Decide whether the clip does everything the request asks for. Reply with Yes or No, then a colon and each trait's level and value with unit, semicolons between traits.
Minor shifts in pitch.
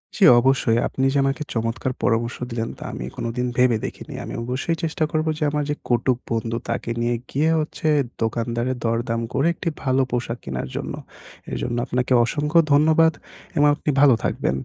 No: average, 3.8 semitones